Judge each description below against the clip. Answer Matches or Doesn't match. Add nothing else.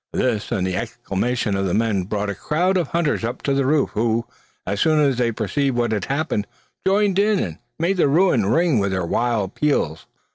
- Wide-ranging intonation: Matches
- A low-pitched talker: Matches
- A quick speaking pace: Matches